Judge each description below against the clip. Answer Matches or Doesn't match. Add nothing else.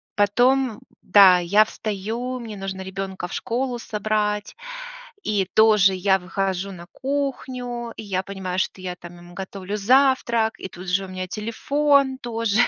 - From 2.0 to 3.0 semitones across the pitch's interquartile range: Doesn't match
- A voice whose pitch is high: Matches